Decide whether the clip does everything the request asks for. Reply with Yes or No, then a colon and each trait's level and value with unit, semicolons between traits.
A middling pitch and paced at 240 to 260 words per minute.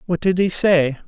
No: medium, 170 Hz; fast, 225 wpm